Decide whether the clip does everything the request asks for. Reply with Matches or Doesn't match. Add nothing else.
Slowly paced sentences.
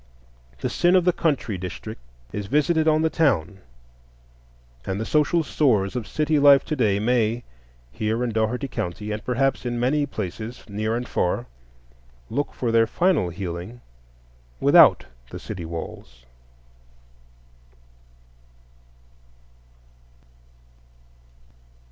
Matches